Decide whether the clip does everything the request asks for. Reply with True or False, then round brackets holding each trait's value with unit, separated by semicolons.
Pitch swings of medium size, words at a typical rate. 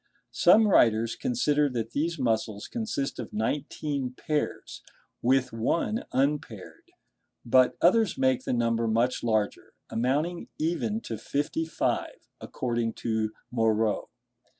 False (5.0 semitones; 115 wpm)